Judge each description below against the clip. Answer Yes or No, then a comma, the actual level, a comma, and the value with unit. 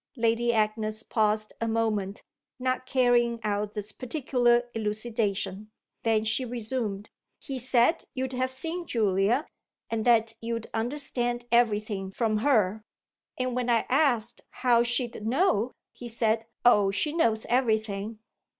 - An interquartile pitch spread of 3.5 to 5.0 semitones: No, narrow, 2.6 semitones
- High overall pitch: Yes, high, 230 Hz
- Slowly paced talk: Yes, slow, 130 wpm